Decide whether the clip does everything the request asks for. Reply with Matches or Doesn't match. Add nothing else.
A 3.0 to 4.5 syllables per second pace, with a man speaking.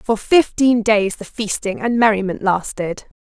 Doesn't match